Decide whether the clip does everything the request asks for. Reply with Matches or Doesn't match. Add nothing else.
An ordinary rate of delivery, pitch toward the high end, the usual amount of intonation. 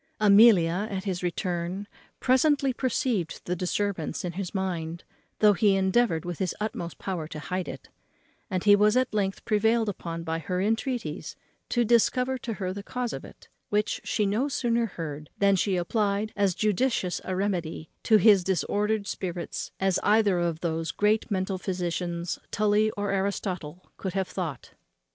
Matches